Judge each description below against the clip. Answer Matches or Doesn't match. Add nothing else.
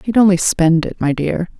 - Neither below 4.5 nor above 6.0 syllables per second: Matches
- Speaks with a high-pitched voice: Doesn't match